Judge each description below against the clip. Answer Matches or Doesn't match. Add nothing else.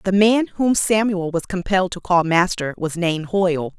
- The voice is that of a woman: Matches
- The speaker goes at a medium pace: Matches